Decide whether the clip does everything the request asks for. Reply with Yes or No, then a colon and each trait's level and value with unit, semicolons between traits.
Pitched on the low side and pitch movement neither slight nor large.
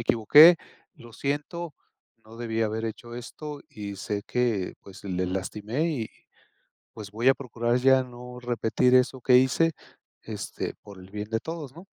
Yes: low, 120 Hz; average, 3.5 semitones